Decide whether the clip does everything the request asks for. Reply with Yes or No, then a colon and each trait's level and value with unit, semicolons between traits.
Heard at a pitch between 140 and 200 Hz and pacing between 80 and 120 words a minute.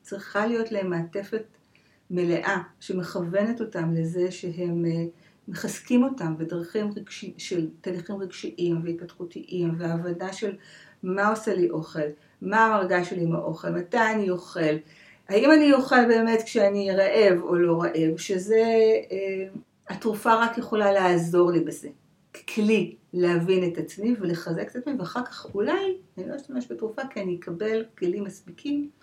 No: high, 190 Hz; average, 140 wpm